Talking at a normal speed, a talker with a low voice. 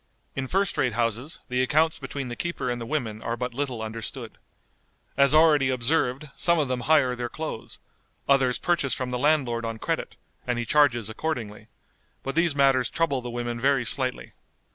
Yes: average, 180 wpm; low, 130 Hz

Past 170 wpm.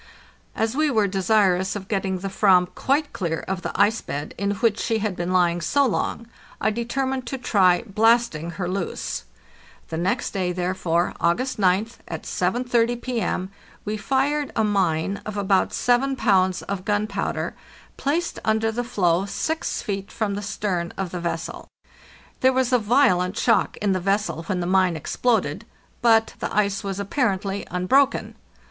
No: average, 165 wpm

